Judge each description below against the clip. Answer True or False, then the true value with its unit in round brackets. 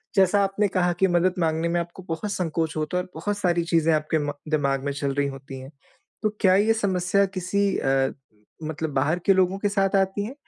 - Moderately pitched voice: True (175 Hz)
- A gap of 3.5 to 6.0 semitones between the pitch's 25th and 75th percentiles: True (3.9 semitones)